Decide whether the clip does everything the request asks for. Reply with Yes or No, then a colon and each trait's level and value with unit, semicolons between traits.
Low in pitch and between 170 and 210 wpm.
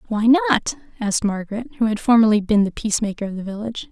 No: high, 215 Hz; average, 200 wpm